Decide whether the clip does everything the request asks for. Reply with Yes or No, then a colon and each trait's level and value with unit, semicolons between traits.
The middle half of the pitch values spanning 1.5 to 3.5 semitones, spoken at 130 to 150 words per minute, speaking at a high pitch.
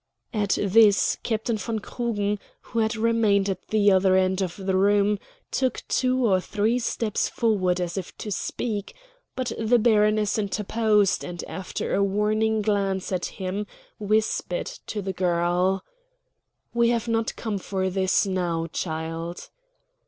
Yes: average, 2.7 semitones; average, 145 wpm; high, 205 Hz